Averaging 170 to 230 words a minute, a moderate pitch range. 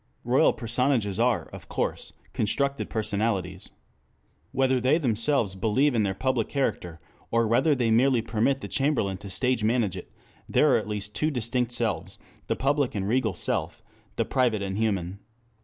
No: average, 160 wpm; average, 4.0 semitones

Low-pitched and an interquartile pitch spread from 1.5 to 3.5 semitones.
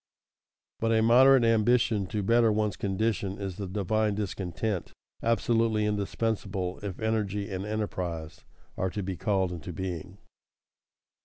Yes: low, 105 Hz; average, 2.8 semitones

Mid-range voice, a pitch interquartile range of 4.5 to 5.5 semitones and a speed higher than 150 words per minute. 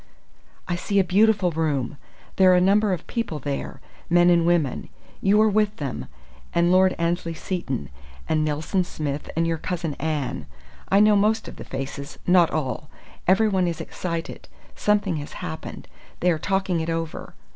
No: medium, 175 Hz; average, 3.7 semitones; average, 165 wpm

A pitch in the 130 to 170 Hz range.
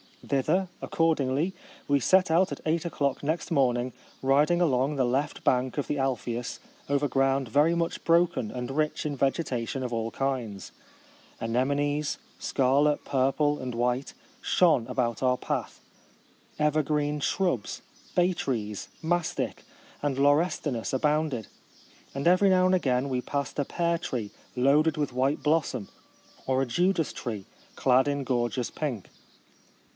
Yes: medium, 140 Hz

